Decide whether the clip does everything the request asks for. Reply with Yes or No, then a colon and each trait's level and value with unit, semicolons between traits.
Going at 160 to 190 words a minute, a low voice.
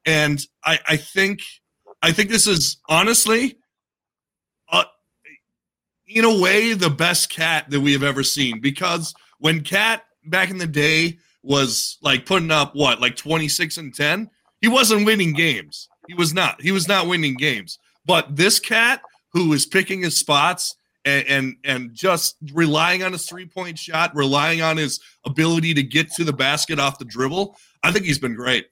No: average, 180 wpm; medium, 165 Hz